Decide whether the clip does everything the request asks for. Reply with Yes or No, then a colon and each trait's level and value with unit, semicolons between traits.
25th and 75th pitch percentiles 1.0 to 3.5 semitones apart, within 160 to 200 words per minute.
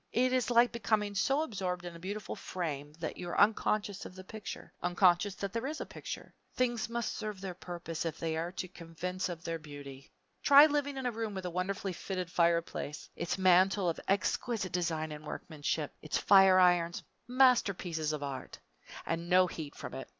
No: average, 4.1 semitones; average, 190 wpm